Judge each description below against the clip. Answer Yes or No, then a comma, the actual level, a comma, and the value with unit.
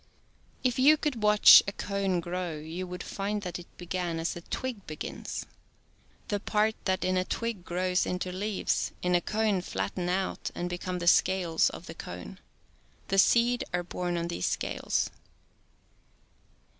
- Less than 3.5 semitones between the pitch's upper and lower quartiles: Yes, average, 2.9 semitones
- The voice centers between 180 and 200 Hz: Yes, medium, 185 Hz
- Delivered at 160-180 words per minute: Yes, average, 170 wpm